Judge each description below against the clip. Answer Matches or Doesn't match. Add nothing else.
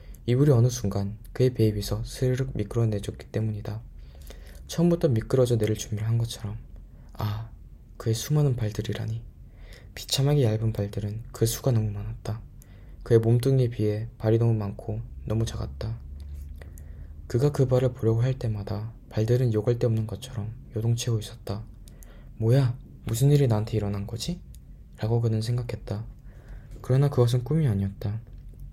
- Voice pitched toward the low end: Matches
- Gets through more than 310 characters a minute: Matches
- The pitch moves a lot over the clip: Doesn't match